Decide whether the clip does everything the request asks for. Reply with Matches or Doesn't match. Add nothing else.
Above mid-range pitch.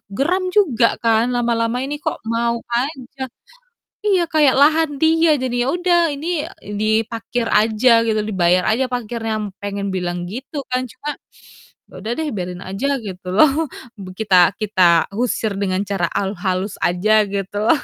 Matches